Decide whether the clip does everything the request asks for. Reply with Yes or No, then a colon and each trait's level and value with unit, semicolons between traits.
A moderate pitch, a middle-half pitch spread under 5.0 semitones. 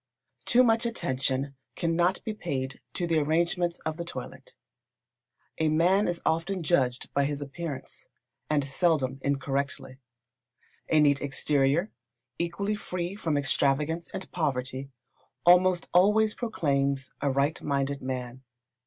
Yes: medium, 155 Hz; average, 4.2 semitones